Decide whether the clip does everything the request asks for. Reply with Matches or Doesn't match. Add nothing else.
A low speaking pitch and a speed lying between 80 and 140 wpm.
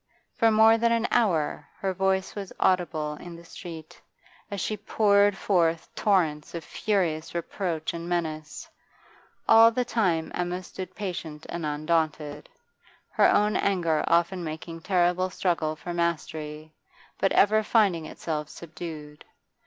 Doesn't match